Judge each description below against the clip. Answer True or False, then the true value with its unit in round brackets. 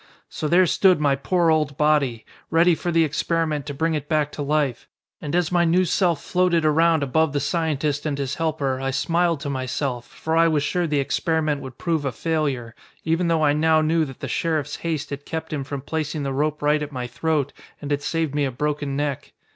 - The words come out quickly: True (220 wpm)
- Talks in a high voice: False (150 Hz)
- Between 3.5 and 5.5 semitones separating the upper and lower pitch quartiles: False (2.5 semitones)